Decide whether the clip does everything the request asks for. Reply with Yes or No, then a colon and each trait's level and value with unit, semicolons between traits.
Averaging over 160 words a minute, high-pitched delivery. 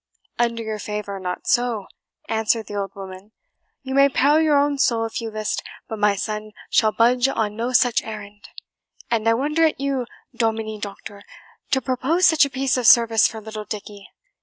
Yes: average, 185 wpm; high, 225 Hz